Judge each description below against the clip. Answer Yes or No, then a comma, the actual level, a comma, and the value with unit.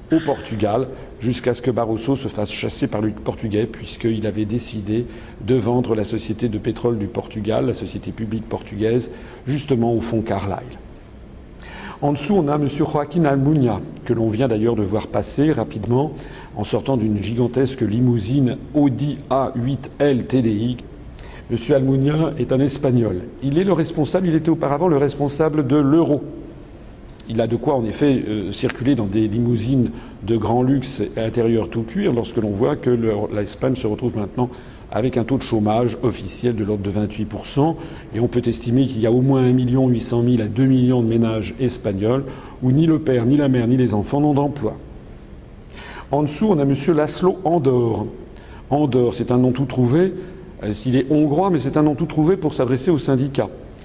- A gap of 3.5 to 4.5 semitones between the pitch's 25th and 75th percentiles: Yes, average, 3.9 semitones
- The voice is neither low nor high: No, low, 125 Hz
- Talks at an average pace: Yes, average, 185 wpm